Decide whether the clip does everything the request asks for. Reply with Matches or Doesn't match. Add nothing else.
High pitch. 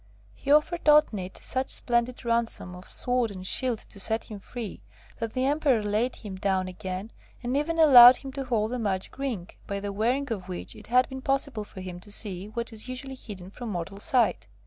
Matches